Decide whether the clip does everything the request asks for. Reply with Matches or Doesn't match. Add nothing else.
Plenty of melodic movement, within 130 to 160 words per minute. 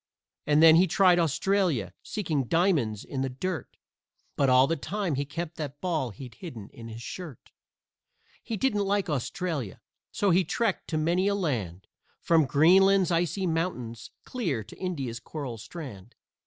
Matches